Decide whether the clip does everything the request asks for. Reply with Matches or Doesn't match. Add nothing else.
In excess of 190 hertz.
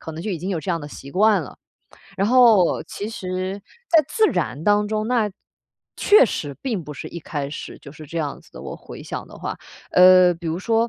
Doesn't match